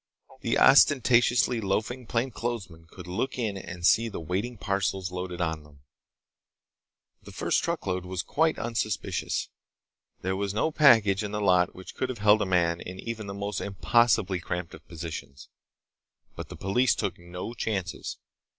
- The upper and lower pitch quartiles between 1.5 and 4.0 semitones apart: No, average, 4.4 semitones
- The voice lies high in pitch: No, low, 100 Hz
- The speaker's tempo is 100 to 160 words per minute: Yes, average, 155 wpm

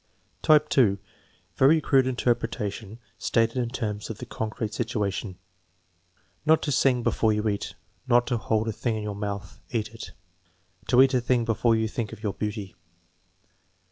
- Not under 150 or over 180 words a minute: Yes, average, 170 wpm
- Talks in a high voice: No, low, 115 Hz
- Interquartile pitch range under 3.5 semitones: Yes, average, 2.7 semitones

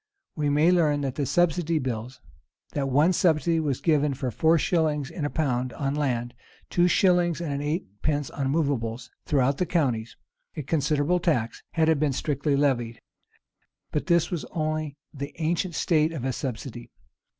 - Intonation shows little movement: No, average, 3.4 semitones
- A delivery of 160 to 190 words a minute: Yes, average, 165 wpm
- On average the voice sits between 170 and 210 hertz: No, medium, 145 Hz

